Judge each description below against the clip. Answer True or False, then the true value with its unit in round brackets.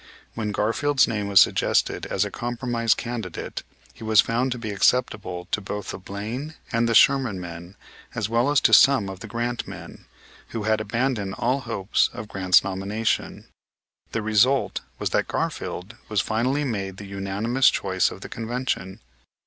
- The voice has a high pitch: False (110 Hz)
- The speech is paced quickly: False (165 wpm)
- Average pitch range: True (3.6 semitones)